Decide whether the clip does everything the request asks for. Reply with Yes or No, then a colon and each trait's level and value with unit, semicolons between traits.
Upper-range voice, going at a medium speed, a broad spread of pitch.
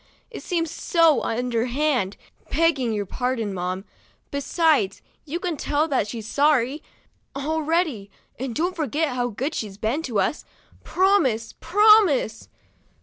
No: very high, 275 Hz; slow, 125 wpm; wide, 6.2 semitones